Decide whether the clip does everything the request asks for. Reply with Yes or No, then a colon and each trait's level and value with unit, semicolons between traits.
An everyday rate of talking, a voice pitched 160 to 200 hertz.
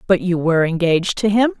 No: fast, 225 wpm; high, 190 Hz